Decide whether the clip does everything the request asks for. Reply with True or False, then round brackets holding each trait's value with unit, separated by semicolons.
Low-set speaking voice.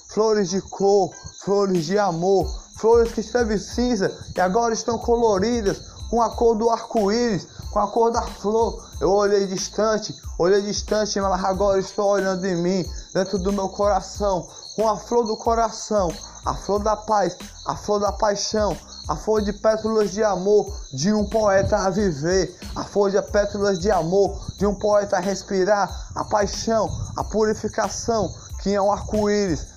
False (205 Hz)